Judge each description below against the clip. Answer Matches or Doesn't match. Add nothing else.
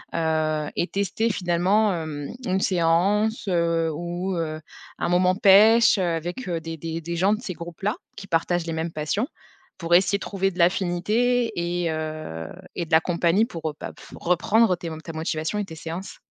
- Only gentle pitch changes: Doesn't match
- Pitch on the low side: Doesn't match